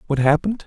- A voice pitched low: No, medium, 165 Hz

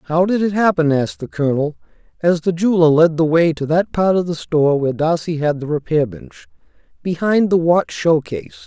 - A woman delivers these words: No, male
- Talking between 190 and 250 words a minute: Yes, average, 200 wpm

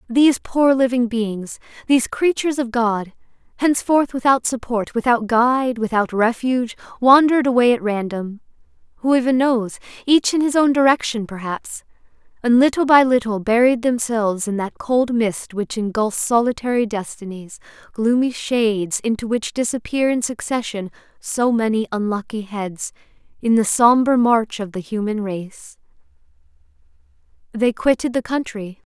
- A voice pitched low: No, high, 235 Hz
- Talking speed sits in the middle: No, slow, 130 wpm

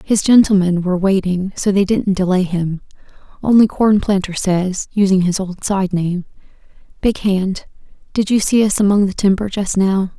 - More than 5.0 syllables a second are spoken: No, 4.8 syllables/s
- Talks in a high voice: Yes, high, 195 Hz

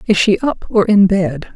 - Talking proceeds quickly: Yes, fast, 230 wpm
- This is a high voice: Yes, high, 195 Hz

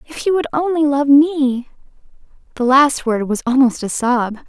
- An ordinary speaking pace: Yes, average, 175 wpm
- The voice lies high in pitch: Yes, very high, 270 Hz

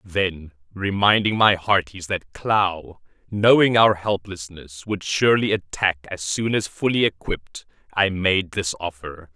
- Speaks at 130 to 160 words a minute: Yes, slow, 135 wpm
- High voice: No, very low, 95 Hz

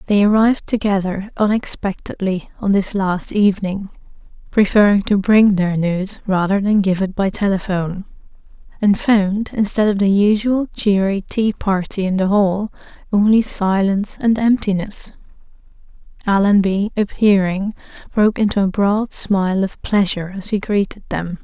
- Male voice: No, female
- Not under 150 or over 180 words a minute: No, slow, 135 wpm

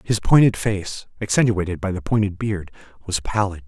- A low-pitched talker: Yes, low, 100 Hz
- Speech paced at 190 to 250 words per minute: No, average, 165 wpm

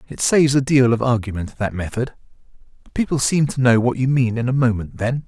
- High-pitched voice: No, low, 125 Hz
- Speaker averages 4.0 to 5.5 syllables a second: No, 5.8 syllables/s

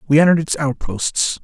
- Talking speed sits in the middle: Yes, average, 165 wpm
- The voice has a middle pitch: Yes, medium, 145 Hz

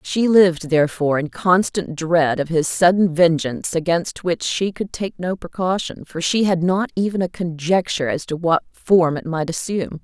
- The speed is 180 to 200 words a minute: Yes, average, 185 wpm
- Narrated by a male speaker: No, female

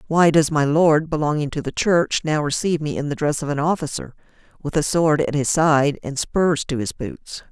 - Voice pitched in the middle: Yes, medium, 150 Hz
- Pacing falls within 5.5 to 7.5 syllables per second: No, 5.0 syllables/s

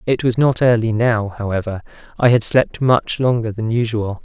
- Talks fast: No, average, 185 wpm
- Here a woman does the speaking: No, male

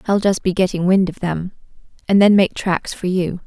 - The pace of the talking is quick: Yes, fast, 225 wpm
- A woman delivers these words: Yes, female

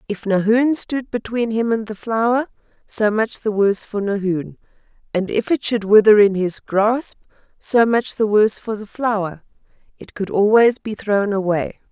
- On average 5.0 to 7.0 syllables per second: No, 4.6 syllables/s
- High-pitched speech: Yes, high, 215 Hz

